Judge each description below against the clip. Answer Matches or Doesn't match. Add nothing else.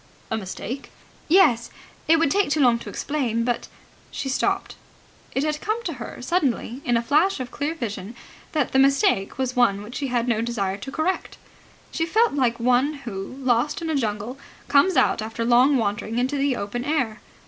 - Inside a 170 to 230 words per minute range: Matches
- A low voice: Doesn't match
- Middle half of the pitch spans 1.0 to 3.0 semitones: Doesn't match